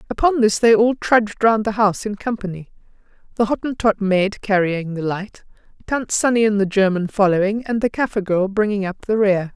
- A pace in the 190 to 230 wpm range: No, average, 180 wpm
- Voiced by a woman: Yes, female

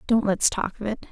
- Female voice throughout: Yes, female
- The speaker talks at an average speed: No, fast, 270 wpm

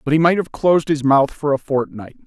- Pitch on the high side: No, medium, 145 Hz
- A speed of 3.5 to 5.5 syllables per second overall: No, 5.8 syllables/s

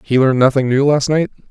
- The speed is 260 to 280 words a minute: No, fast, 240 wpm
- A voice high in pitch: No, low, 135 Hz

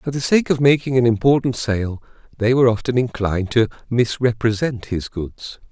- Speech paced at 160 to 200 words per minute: Yes, average, 170 wpm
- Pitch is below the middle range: Yes, low, 120 Hz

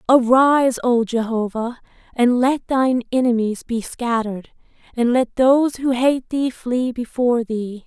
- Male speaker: No, female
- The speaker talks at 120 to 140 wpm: Yes, slow, 135 wpm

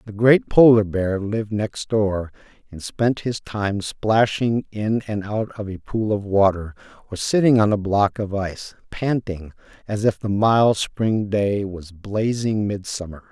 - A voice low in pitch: Yes, low, 105 Hz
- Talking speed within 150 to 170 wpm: Yes, average, 165 wpm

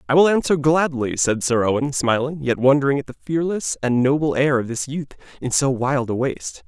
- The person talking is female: No, male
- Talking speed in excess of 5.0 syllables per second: Yes, 5.5 syllables/s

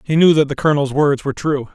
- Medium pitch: Yes, medium, 145 Hz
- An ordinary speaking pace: No, fast, 275 wpm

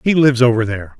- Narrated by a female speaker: No, male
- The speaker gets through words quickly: Yes, fast, 240 wpm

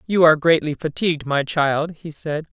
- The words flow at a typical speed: Yes, average, 185 wpm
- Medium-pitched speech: Yes, medium, 155 Hz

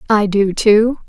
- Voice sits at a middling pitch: No, high, 210 Hz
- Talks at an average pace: Yes, average, 165 wpm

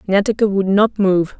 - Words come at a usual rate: Yes, average, 170 wpm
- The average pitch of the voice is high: Yes, high, 200 Hz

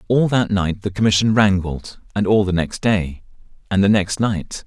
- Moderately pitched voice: No, low, 100 Hz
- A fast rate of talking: No, average, 195 wpm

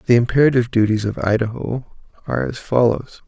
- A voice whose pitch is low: Yes, low, 120 Hz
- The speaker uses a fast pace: No, average, 145 wpm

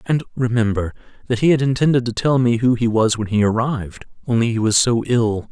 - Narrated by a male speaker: Yes, male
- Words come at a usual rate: No, fast, 215 wpm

